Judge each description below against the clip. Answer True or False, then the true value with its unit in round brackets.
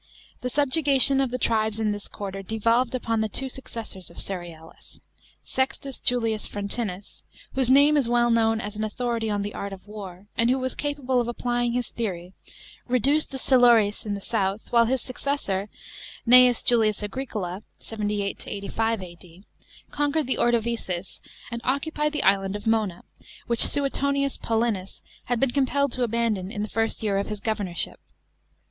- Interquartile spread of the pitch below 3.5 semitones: False (3.8 semitones)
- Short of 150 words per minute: False (165 wpm)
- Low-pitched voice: False (230 Hz)